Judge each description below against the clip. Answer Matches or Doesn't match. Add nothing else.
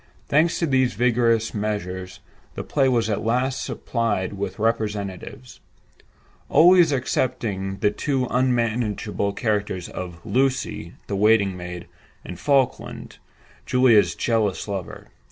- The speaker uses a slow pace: Matches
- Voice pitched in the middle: Doesn't match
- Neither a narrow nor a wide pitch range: Matches